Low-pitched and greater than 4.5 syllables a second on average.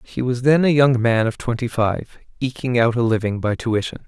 Yes: low, 120 Hz; 5.1 syllables/s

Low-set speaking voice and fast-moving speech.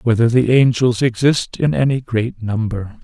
No: low, 120 Hz; average, 160 wpm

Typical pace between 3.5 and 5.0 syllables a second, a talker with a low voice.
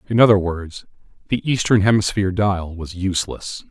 No: 5.3 syllables/s; low, 100 Hz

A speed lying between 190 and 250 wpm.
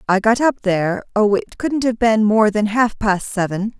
Yes: fast, 205 wpm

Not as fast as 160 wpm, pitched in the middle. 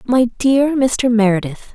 No: average, 140 wpm; high, 240 Hz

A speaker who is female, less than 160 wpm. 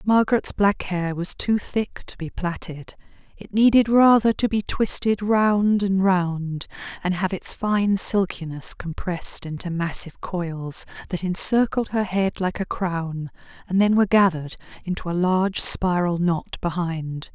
Yes: female; average, 150 wpm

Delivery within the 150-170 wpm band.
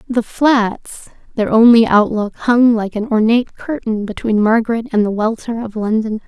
Yes: average, 160 wpm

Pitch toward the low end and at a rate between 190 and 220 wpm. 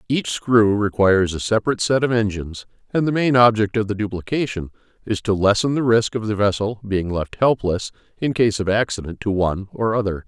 Yes: low, 105 Hz; average, 200 wpm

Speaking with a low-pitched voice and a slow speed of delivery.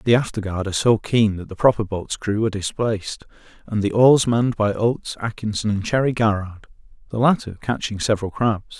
No: low, 110 Hz; average, 190 wpm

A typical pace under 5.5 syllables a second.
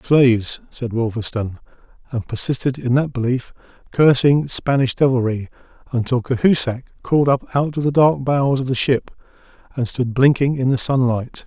Yes: 5.2 syllables/s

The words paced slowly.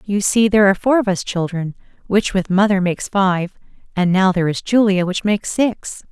No: fast, 205 wpm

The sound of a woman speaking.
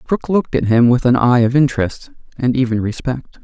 No: male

